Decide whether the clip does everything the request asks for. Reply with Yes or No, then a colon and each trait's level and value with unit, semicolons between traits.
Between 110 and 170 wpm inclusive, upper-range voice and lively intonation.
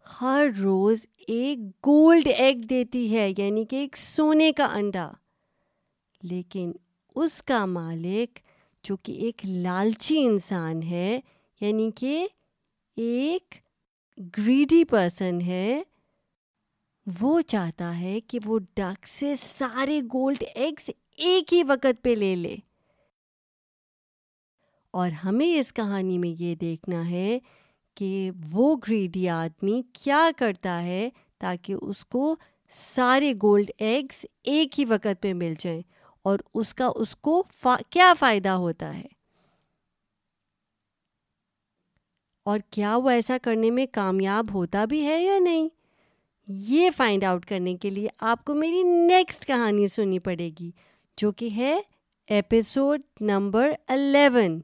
Yes: average, 125 wpm; high, 225 Hz; wide, 6.0 semitones